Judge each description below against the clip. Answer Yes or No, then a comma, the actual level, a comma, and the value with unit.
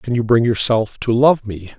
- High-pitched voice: No, low, 115 Hz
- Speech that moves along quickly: Yes, fast, 235 wpm